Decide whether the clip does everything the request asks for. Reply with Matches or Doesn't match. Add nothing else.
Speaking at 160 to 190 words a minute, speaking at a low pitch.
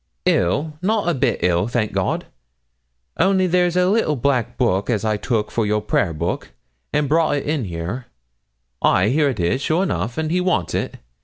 Matches